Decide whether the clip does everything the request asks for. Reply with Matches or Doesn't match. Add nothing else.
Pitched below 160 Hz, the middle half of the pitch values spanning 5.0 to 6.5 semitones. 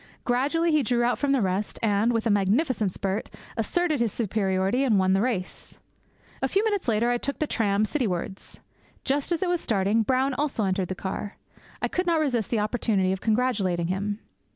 Doesn't match